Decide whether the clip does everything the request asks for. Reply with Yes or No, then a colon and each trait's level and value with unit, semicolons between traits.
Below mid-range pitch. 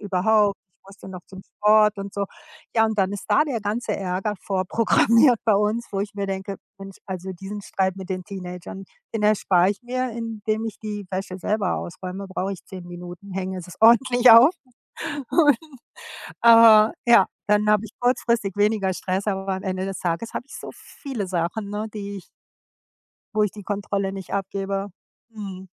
No: high, 200 Hz